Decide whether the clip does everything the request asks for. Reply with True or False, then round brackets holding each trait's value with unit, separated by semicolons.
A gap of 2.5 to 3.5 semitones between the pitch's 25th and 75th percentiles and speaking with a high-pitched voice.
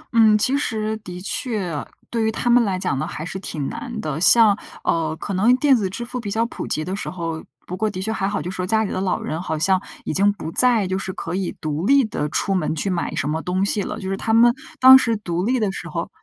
False (3.9 semitones; 195 Hz)